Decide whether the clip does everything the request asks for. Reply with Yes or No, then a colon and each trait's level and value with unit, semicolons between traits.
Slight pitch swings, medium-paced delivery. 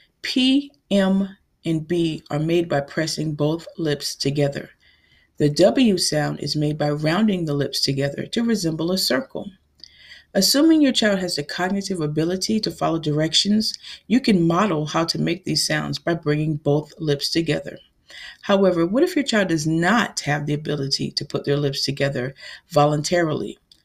No: average, 4.8 semitones; average, 160 wpm